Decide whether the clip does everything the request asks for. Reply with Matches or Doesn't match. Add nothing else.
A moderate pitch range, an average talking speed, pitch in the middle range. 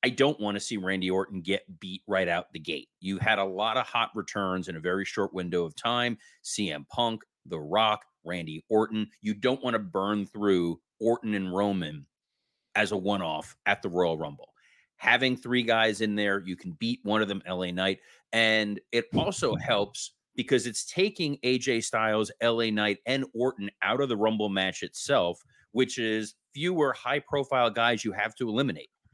Doesn't match